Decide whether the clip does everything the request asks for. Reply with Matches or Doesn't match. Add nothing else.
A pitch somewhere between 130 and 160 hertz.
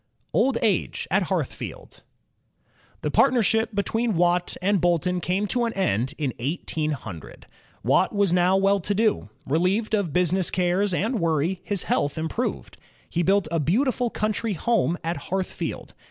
Doesn't match